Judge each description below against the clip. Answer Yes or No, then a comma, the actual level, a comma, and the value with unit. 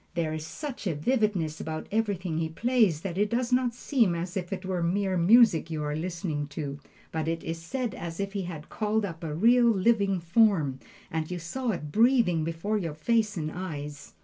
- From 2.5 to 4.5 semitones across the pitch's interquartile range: No, average, 5.1 semitones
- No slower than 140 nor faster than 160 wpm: No, average, 200 wpm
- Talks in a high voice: No, medium, 180 Hz